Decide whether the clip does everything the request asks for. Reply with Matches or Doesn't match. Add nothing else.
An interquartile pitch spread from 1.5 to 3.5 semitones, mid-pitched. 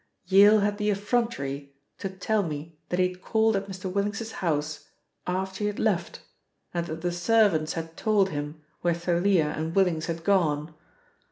Doesn't match